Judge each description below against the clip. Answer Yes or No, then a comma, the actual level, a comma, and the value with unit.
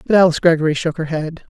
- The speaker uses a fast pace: Yes, fast, 230 wpm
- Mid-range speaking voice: Yes, medium, 160 Hz